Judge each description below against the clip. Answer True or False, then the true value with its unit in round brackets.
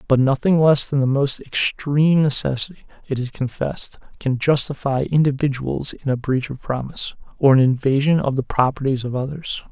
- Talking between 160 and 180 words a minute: True (165 wpm)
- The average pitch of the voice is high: False (140 Hz)